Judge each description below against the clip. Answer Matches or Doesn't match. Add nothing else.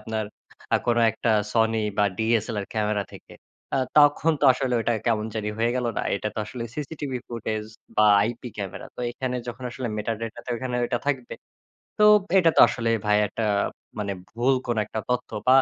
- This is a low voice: Matches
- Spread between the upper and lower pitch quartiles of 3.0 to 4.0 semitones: Doesn't match